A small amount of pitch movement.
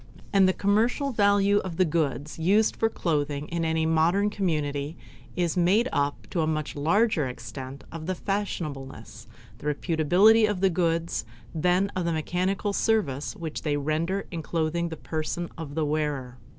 No: average, 4.3 semitones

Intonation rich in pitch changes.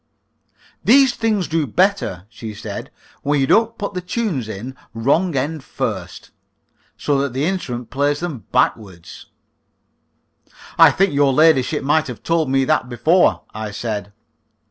Yes: wide, 6.5 semitones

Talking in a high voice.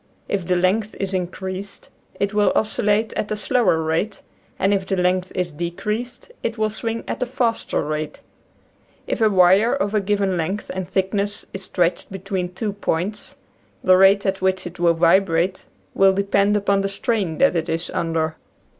Yes: high, 195 Hz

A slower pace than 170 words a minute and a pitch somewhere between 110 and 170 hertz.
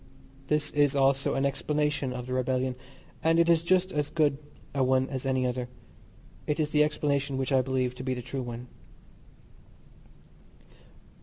Yes: average, 160 wpm; low, 135 Hz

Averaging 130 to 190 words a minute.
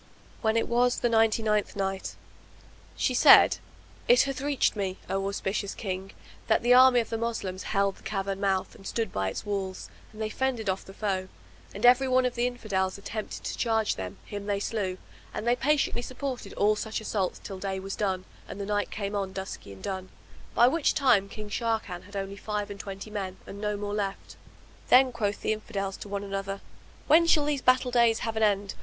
No: fast, 205 wpm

